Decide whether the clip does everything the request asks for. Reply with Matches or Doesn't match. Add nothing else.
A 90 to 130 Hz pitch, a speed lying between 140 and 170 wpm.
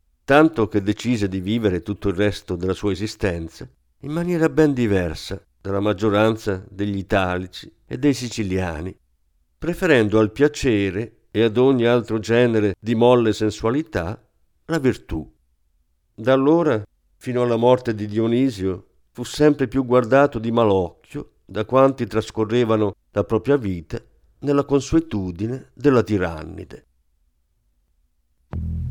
Doesn't match